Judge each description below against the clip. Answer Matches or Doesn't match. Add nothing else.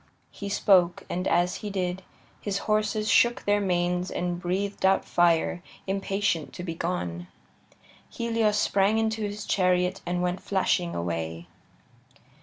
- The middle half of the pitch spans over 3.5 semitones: Doesn't match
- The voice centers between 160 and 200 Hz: Matches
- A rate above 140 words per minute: Doesn't match